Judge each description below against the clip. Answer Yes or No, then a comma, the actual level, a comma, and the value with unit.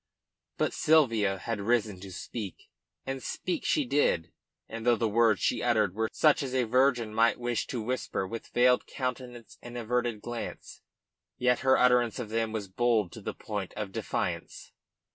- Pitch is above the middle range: No, low, 115 Hz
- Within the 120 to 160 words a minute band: No, average, 170 wpm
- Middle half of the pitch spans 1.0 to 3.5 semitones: Yes, narrow, 2.5 semitones